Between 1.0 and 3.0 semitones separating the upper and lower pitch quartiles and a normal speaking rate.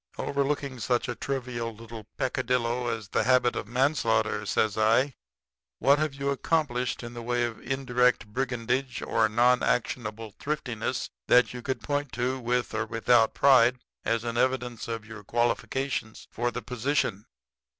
Yes: narrow, 2.4 semitones; average, 150 wpm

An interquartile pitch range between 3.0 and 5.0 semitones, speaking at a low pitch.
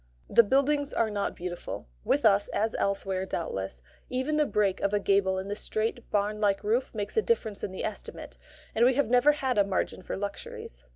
No: average, 4.3 semitones; high, 210 Hz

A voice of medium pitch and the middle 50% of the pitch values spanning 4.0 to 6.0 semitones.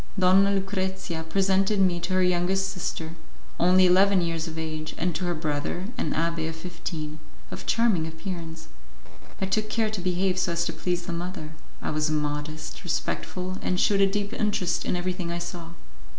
No: medium, 180 Hz; average, 2.7 semitones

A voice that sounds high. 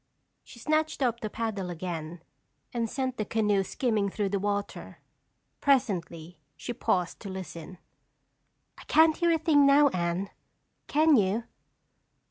Yes: high, 210 Hz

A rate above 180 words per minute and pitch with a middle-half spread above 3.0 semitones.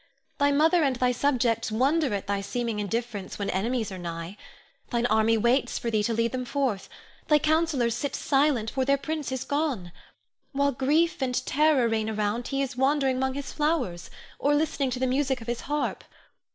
Yes: average, 190 wpm; average, 4.1 semitones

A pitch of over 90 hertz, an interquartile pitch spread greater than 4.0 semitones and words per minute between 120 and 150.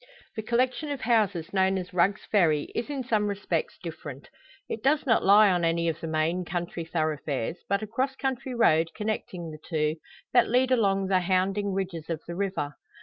No: high, 190 Hz; average, 4.9 semitones; average, 190 wpm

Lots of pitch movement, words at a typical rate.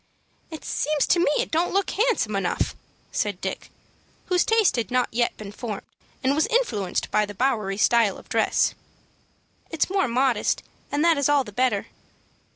Yes: wide, 7.4 semitones; average, 170 wpm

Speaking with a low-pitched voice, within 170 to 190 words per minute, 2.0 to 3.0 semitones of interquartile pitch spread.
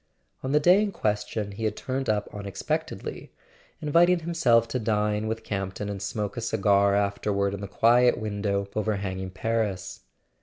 Yes: low, 105 Hz; average, 175 wpm; average, 2.7 semitones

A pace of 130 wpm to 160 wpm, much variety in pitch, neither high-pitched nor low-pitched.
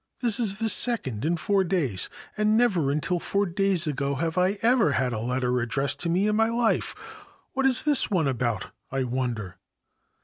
No: average, 180 wpm; wide, 8.3 semitones; medium, 170 Hz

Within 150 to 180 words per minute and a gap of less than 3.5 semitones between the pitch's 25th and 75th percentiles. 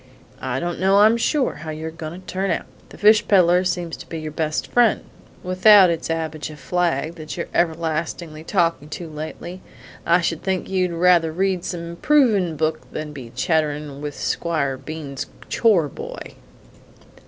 Yes: average, 165 wpm; average, 2.8 semitones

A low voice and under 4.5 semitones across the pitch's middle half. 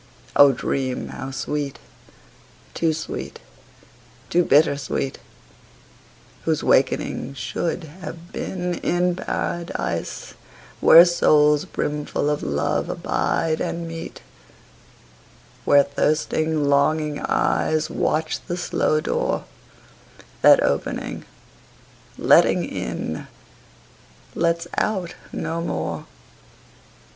No: medium, 155 Hz; average, 2.9 semitones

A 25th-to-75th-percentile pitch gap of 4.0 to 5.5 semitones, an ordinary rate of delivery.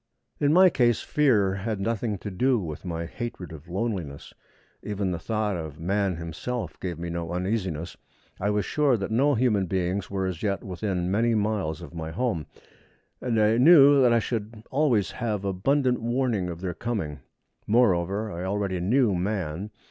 Yes: average, 4.7 semitones; average, 170 wpm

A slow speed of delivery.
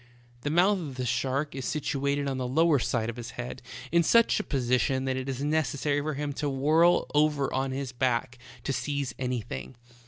No: fast, 205 wpm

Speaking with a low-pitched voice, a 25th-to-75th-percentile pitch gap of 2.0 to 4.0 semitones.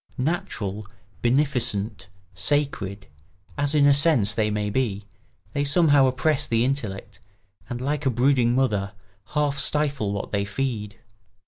No: low, 125 Hz; average, 5.3 semitones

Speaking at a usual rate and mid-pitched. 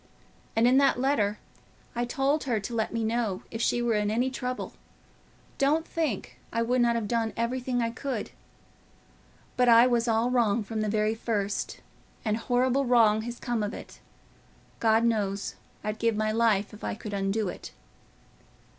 No: average, 170 wpm; high, 230 Hz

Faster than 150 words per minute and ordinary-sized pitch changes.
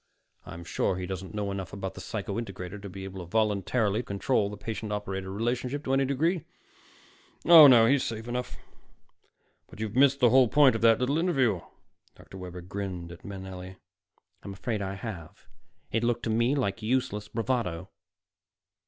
Yes: average, 170 wpm; average, 4.6 semitones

